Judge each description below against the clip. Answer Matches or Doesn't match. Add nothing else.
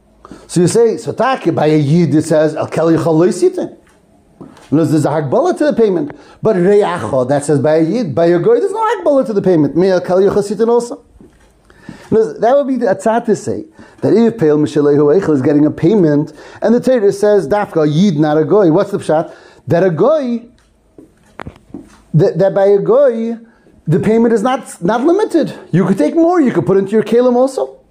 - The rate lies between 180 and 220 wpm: Matches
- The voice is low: Doesn't match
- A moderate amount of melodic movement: Doesn't match